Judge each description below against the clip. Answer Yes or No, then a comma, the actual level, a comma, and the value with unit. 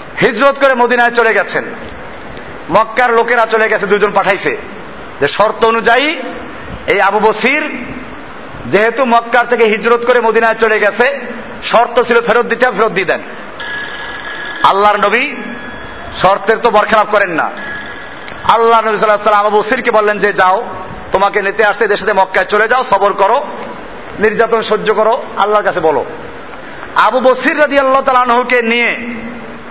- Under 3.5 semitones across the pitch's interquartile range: Yes, average, 2.7 semitones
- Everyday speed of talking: No, fast, 125 wpm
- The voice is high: Yes, high, 225 Hz